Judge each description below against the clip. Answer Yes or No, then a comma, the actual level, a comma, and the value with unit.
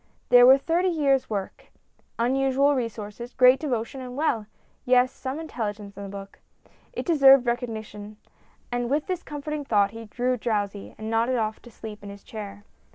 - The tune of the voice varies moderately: Yes, average, 4.1 semitones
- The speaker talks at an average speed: Yes, average, 165 wpm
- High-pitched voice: Yes, high, 245 Hz